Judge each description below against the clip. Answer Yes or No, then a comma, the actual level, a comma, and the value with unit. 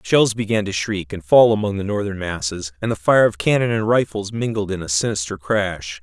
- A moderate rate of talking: No, fast, 220 wpm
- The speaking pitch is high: No, low, 100 Hz